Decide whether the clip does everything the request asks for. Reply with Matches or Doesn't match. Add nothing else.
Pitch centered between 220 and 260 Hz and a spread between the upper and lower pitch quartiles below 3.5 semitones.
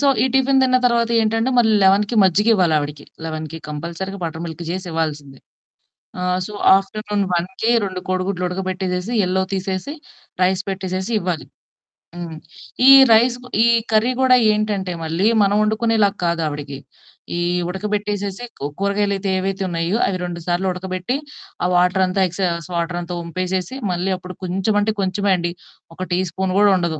Doesn't match